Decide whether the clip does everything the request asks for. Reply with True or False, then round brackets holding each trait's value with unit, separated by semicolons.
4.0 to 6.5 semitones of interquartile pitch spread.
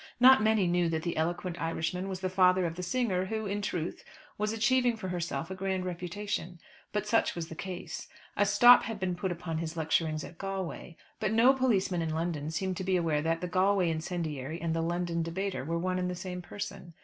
False (2.8 semitones)